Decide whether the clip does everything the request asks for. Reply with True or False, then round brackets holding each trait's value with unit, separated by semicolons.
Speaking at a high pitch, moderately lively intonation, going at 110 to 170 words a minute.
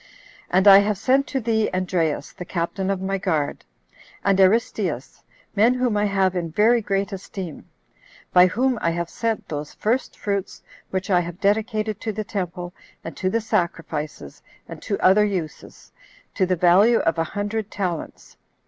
True (195 Hz; 3.2 semitones; 165 wpm)